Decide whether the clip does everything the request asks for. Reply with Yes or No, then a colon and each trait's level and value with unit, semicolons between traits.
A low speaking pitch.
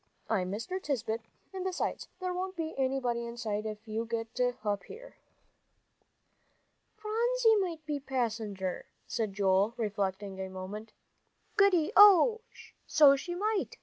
No: high, 240 Hz